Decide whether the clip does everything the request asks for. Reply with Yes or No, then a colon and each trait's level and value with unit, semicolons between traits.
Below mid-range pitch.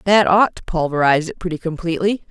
No: medium, 175 Hz